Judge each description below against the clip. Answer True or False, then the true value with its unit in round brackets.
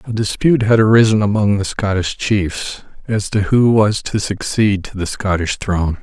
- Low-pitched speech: True (105 Hz)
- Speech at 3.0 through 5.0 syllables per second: True (4.8 syllables/s)